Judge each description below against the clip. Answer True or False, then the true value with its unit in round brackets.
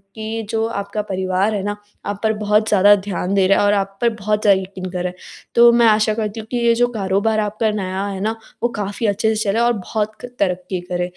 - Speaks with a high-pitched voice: True (205 Hz)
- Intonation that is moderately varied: False (2.3 semitones)